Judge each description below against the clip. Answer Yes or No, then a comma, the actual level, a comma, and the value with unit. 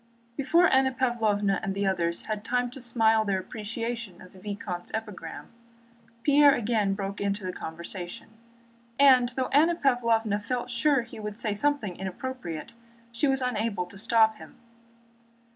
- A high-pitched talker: Yes, high, 220 Hz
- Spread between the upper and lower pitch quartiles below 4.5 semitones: Yes, average, 4.1 semitones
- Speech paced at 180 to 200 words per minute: No, average, 150 wpm